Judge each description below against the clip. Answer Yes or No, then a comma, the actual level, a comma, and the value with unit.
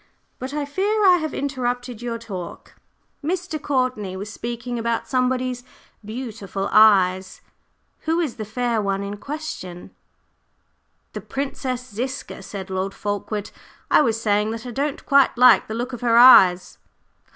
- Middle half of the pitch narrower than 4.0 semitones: No, average, 4.3 semitones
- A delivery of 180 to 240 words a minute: No, average, 145 wpm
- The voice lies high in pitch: Yes, high, 240 Hz